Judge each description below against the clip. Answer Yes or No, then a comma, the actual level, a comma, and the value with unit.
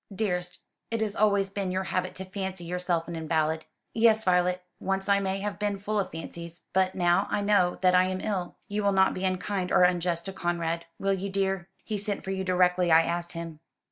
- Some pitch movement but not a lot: No, narrow, 2.1 semitones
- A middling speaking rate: No, fast, 215 wpm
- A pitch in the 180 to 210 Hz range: Yes, medium, 185 Hz